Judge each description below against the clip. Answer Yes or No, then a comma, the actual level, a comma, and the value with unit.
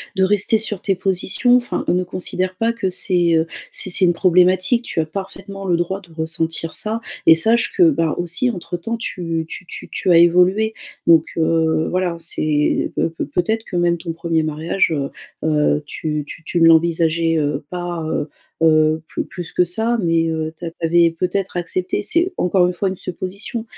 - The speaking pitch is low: No, medium, 175 Hz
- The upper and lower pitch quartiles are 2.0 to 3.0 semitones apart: Yes, average, 2.7 semitones